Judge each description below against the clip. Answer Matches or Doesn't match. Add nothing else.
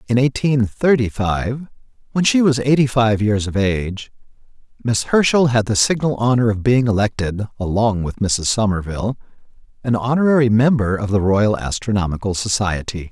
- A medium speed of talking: Matches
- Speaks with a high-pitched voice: Doesn't match